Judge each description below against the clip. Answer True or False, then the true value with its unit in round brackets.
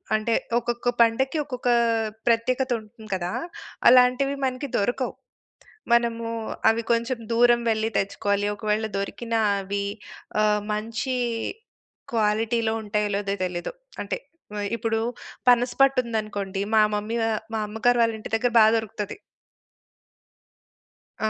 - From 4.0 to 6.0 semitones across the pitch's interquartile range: False (2.5 semitones)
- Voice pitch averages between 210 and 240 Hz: True (225 Hz)